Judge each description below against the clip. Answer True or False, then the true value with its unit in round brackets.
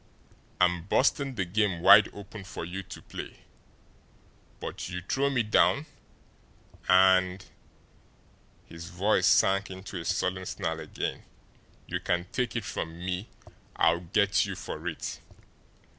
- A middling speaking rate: False (130 wpm)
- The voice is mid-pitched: False (95 Hz)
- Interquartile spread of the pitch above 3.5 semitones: False (2.6 semitones)